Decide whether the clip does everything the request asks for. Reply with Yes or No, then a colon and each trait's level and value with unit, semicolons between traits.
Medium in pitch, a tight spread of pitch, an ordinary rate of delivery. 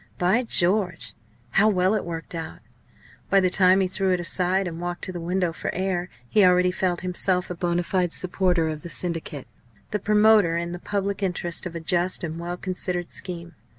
Yes: medium, 180 Hz; narrow, 1.6 semitones; average, 195 wpm